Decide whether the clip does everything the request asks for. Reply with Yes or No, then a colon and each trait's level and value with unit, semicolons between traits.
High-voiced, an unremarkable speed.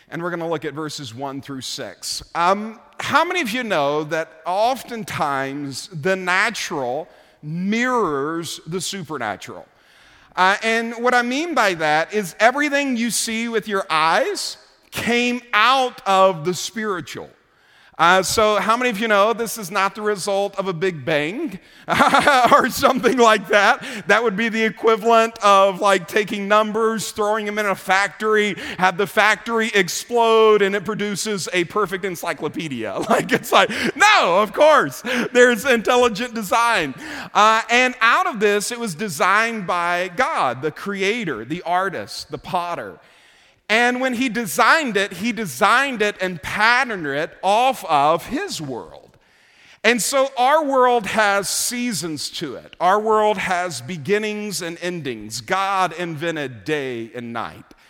Yes: high, 205 Hz; average, 150 wpm